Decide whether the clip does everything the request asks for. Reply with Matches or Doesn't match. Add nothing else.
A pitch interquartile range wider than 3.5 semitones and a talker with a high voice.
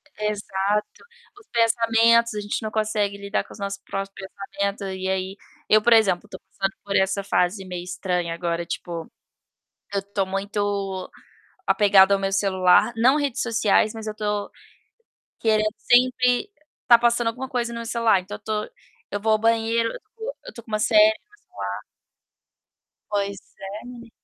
Doesn't match